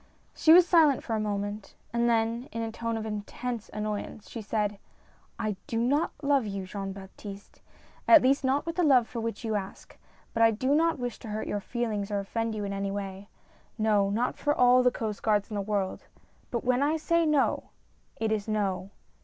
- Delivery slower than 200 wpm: No, fast, 205 wpm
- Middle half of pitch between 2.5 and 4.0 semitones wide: Yes, average, 3.5 semitones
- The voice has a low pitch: No, high, 225 Hz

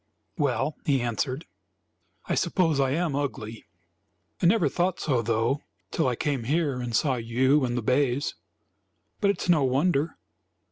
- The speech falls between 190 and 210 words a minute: No, average, 155 wpm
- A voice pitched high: No, low, 135 Hz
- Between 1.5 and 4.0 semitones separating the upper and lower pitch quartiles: No, average, 4.4 semitones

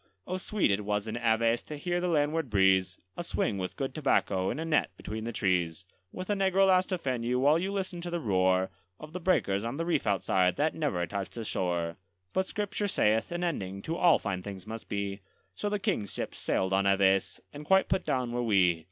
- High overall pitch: No, low, 115 Hz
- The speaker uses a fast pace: Yes, fast, 225 wpm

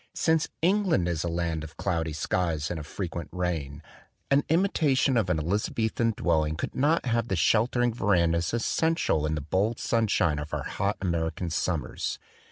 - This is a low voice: Yes, very low, 90 Hz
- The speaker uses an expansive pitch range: Yes, wide, 6.3 semitones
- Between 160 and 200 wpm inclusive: Yes, average, 170 wpm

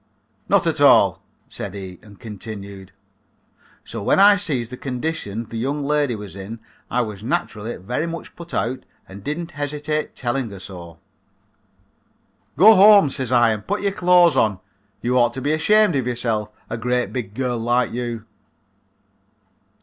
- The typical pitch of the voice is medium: No, low, 125 Hz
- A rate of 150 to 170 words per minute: Yes, average, 165 wpm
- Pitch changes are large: Yes, wide, 5.7 semitones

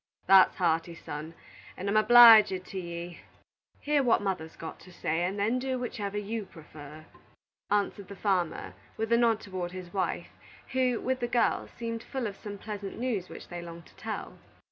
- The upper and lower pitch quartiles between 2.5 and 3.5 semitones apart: No, average, 4.8 semitones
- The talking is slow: No, average, 180 wpm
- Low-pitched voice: No, high, 200 Hz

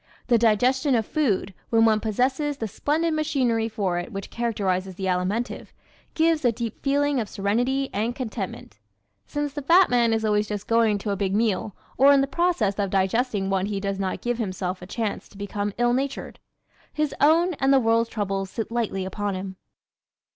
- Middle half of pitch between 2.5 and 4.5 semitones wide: No, average, 4.9 semitones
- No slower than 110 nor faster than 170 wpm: No, average, 190 wpm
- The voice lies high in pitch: Yes, high, 225 Hz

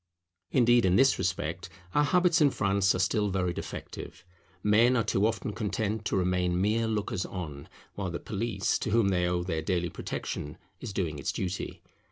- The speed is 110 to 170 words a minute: No, average, 180 wpm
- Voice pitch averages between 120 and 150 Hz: No, very low, 95 Hz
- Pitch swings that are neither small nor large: Yes, average, 3.7 semitones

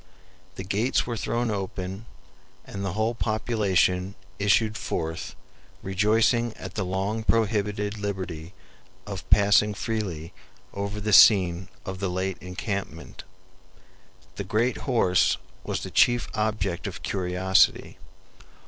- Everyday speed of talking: No, slow, 115 wpm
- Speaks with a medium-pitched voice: No, low, 100 Hz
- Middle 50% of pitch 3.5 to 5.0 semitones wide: No, average, 2.7 semitones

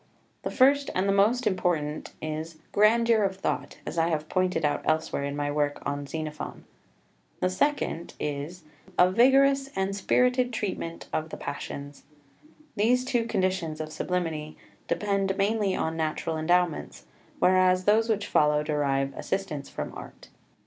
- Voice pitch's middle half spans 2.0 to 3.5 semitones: No, average, 5.2 semitones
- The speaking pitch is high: No, medium, 180 Hz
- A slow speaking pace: No, average, 150 wpm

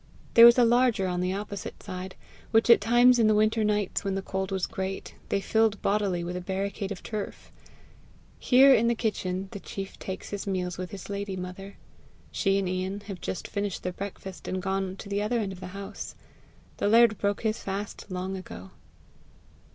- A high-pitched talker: Yes, high, 200 Hz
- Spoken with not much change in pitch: Yes, narrow, 2.2 semitones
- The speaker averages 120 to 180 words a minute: No, average, 195 wpm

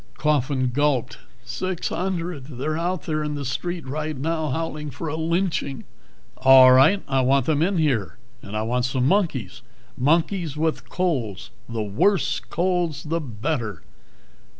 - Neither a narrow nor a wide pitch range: Yes, average, 4.3 semitones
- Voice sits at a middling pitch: Yes, medium, 150 Hz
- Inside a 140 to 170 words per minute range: Yes, average, 150 wpm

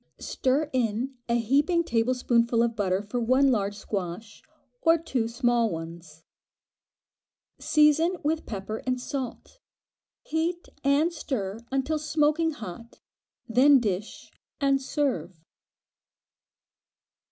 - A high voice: Yes, very high, 250 Hz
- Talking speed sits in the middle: No, slow, 105 wpm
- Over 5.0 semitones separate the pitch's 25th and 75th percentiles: Yes, wide, 5.5 semitones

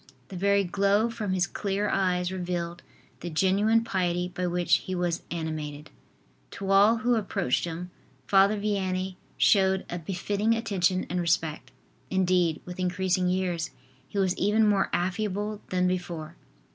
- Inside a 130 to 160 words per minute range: Yes, average, 145 wpm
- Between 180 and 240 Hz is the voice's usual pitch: Yes, medium, 185 Hz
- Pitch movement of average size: No, narrow, 2.3 semitones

